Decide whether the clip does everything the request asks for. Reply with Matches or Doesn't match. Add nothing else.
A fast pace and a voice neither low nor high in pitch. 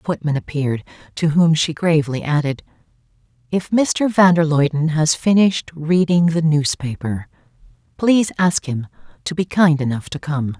Doesn't match